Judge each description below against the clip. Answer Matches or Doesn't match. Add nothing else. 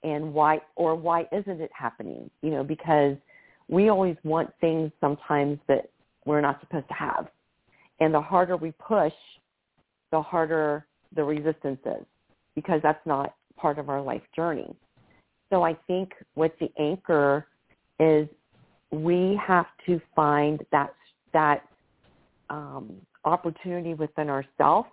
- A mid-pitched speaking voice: Matches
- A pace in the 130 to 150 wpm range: Matches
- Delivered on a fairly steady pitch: Matches